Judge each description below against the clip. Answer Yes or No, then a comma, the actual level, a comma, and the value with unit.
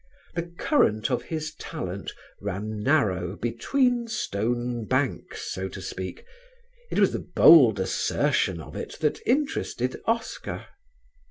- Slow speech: Yes, slow, 120 wpm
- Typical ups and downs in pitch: No, wide, 8.8 semitones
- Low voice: Yes, low, 120 Hz